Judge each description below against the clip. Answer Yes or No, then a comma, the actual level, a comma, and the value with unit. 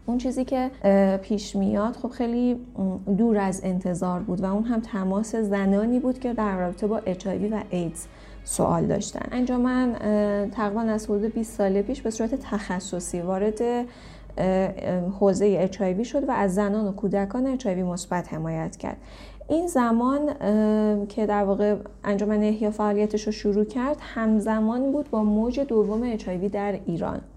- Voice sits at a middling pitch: No, high, 210 Hz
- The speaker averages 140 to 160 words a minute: Yes, average, 150 wpm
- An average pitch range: Yes, average, 3.2 semitones